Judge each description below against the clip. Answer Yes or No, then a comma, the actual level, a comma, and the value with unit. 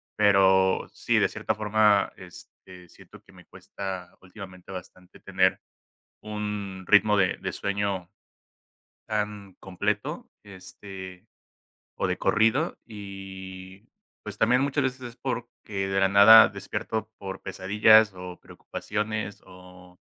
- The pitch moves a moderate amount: No, narrow, 2.3 semitones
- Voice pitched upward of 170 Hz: No, low, 100 Hz